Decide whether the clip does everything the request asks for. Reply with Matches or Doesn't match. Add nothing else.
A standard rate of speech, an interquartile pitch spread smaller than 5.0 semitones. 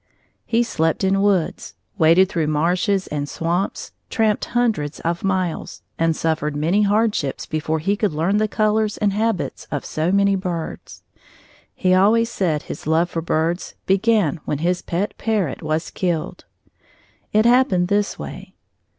Matches